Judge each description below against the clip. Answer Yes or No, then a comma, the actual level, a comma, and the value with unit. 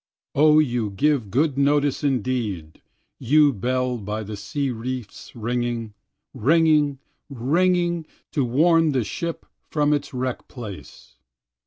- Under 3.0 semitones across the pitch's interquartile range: No, average, 4.3 semitones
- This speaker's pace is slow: Yes, slow, 120 wpm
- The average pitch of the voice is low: Yes, low, 130 Hz